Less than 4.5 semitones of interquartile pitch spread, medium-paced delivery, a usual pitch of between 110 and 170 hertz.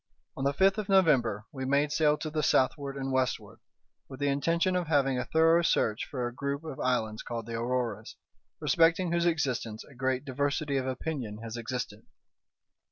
Yes: average, 4.0 semitones; average, 180 wpm; low, 135 Hz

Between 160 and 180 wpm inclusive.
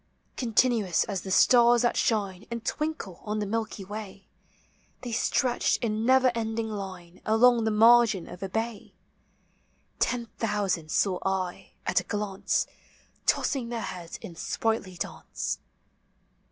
No: slow, 135 wpm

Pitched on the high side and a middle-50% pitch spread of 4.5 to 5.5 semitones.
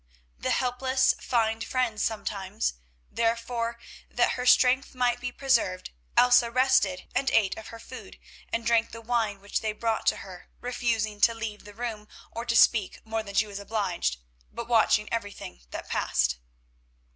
No: high, 225 Hz; average, 2.8 semitones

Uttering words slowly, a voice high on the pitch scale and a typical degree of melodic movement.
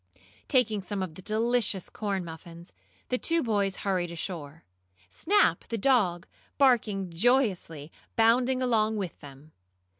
No: slow, 125 wpm; high, 200 Hz; wide, 5.7 semitones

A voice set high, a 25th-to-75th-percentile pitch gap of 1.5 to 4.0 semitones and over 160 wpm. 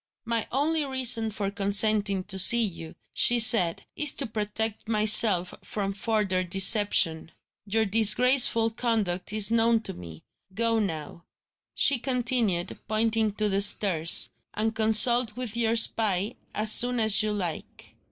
No: high, 215 Hz; narrow, 2.6 semitones; average, 140 wpm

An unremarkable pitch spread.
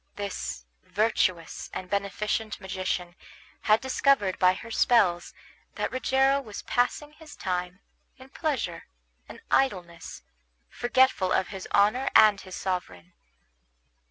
No: wide, 5.8 semitones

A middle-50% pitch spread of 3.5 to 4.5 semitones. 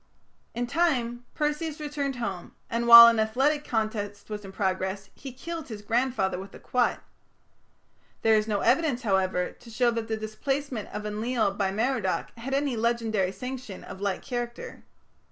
Yes: average, 3.9 semitones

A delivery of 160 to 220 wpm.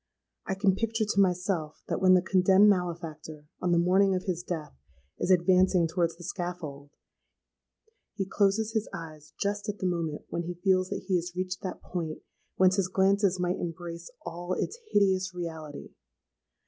Yes: average, 170 wpm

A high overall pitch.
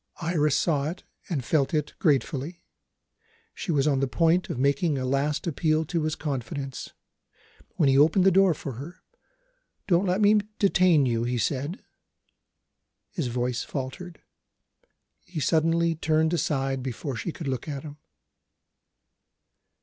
No: medium, 150 Hz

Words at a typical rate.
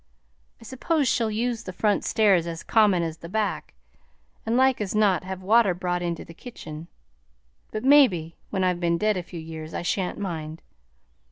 Yes: average, 180 wpm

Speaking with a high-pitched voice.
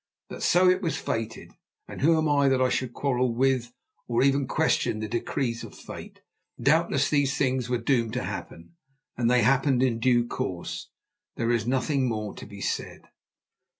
No: low, 130 Hz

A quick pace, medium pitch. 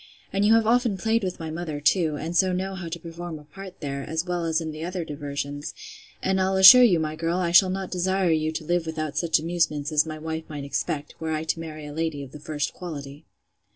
Yes: fast, 245 wpm; medium, 165 Hz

